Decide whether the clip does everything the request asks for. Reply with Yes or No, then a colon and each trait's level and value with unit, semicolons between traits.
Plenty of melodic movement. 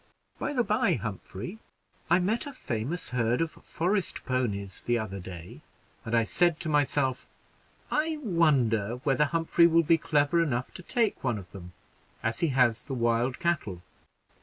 Yes: wide, 6.9 semitones